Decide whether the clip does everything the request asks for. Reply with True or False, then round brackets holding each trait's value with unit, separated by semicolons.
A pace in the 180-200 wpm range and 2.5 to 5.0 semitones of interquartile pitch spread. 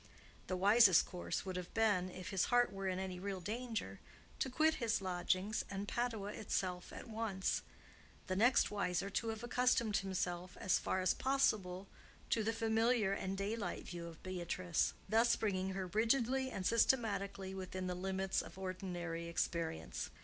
False (155 wpm; 3.4 semitones)